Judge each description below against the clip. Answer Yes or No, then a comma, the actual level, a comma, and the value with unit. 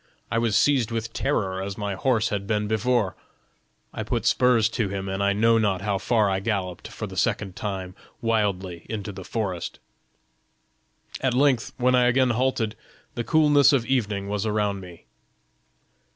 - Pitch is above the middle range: No, low, 110 Hz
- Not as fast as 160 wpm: No, average, 165 wpm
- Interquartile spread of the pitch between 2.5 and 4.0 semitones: Yes, average, 3.3 semitones